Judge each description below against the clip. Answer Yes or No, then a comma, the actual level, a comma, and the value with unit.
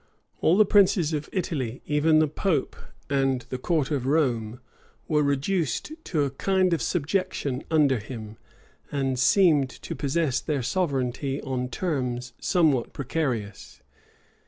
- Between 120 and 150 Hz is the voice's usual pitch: Yes, medium, 140 Hz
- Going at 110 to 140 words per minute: Yes, slow, 135 wpm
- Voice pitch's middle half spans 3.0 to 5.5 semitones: Yes, average, 4.2 semitones